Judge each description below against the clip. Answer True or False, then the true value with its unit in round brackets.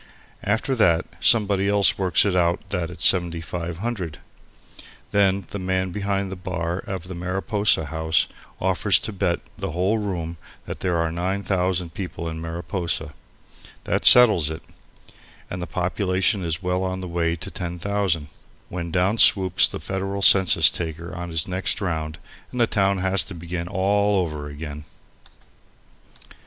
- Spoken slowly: False (150 wpm)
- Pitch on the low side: True (90 Hz)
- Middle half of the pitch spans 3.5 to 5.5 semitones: False (2.6 semitones)